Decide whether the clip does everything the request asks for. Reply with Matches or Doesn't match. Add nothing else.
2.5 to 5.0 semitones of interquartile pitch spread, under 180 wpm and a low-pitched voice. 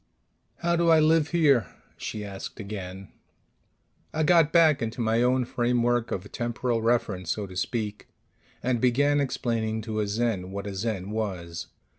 Matches